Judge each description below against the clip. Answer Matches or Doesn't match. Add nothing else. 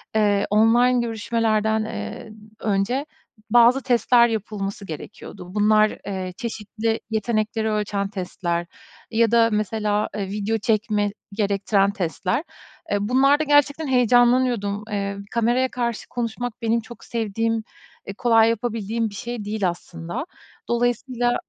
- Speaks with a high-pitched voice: Matches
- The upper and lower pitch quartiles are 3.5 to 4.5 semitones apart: Doesn't match